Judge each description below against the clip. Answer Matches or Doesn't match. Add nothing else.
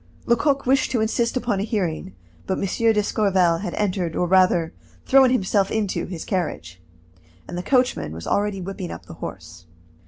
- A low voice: Doesn't match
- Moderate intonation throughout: Matches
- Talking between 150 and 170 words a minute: Matches